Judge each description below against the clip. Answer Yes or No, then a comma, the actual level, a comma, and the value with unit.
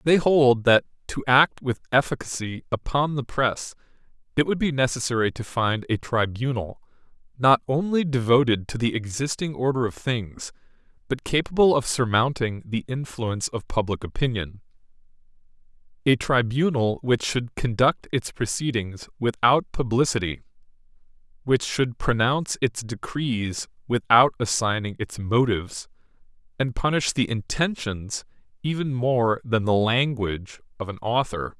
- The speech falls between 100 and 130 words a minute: Yes, slow, 125 wpm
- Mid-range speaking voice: No, low, 125 Hz